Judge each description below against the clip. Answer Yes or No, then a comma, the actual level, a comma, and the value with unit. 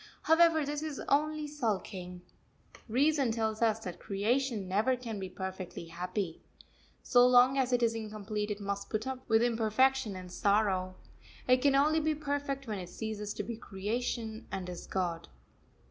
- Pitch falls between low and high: No, high, 225 Hz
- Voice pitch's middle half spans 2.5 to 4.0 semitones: No, average, 5.1 semitones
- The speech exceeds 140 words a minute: Yes, average, 160 wpm